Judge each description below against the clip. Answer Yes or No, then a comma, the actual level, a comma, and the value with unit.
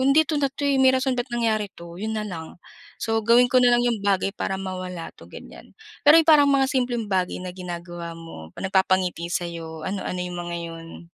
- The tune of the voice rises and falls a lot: Yes, wide, 6.2 semitones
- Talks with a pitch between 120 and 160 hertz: No, high, 195 Hz